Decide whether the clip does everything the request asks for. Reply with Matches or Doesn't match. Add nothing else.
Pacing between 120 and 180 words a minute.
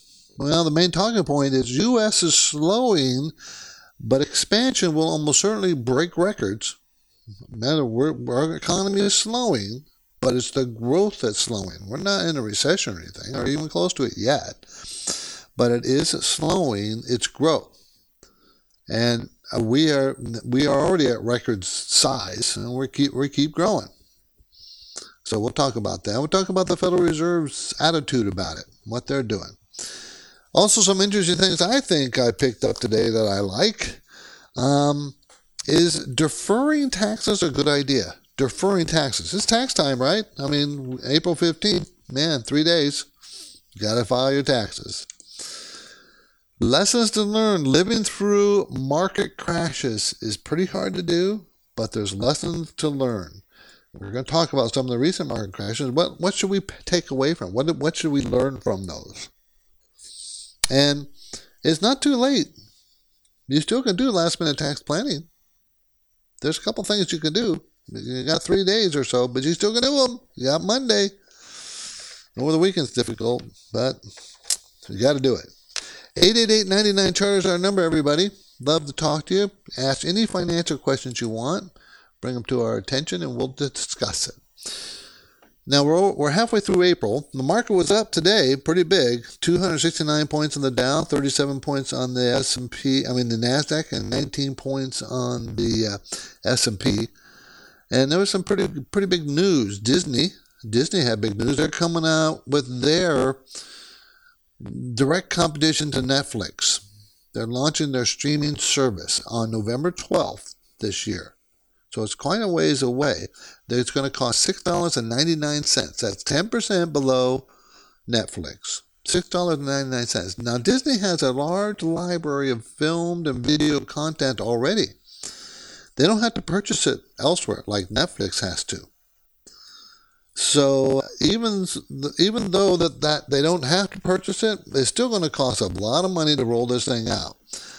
Matches